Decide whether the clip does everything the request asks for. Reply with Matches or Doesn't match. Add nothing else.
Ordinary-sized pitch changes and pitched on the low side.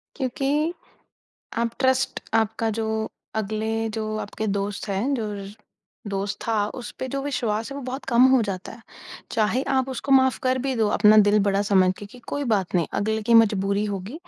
Doesn't match